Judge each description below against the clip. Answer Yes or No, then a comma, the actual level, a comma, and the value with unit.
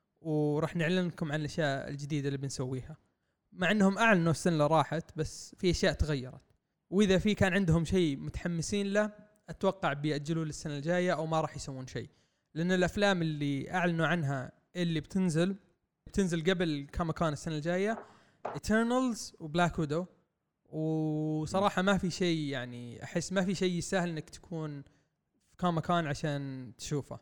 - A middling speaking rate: No, fast, 140 wpm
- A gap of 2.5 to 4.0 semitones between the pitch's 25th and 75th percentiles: Yes, average, 3.7 semitones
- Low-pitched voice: No, medium, 165 Hz